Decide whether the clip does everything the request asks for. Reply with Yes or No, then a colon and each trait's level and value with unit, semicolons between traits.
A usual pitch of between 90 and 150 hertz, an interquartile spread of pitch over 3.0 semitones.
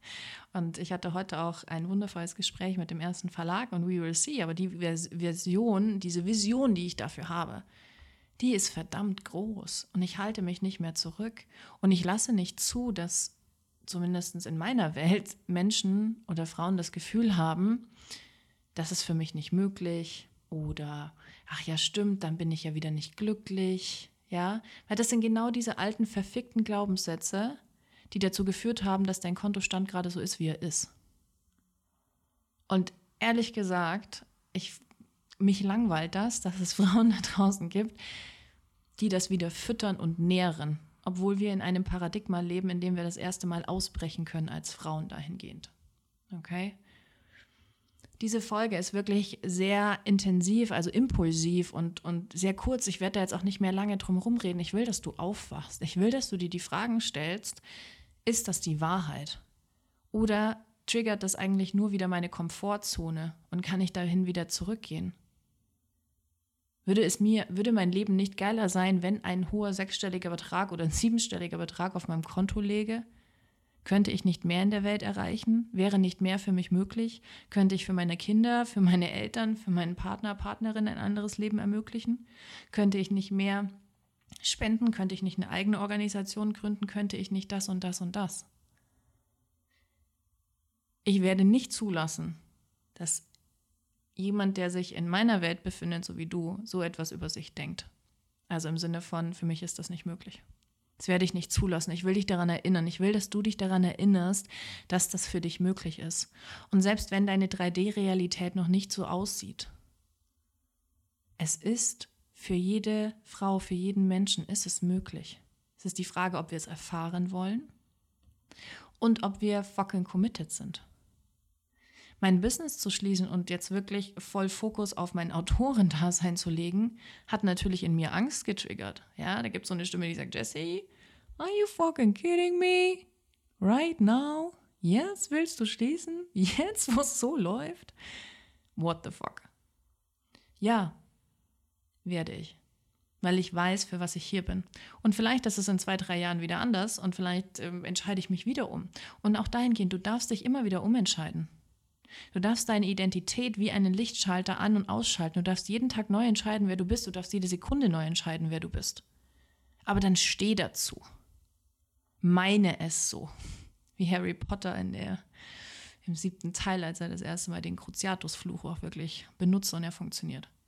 No: medium, 185 Hz; average, 3.4 semitones